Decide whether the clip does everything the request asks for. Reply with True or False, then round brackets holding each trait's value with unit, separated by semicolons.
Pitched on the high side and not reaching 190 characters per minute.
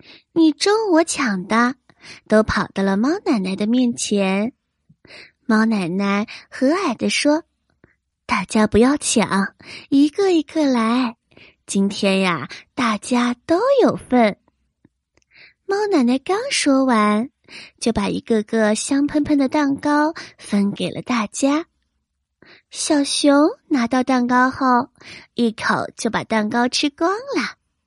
True (250 Hz; 170 characters per minute)